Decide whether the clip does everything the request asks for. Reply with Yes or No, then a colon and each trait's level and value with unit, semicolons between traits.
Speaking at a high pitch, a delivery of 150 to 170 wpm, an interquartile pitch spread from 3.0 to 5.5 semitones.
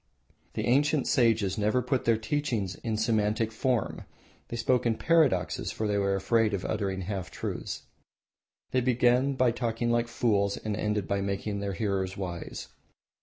No: low, 110 Hz; average, 160 wpm; average, 3.3 semitones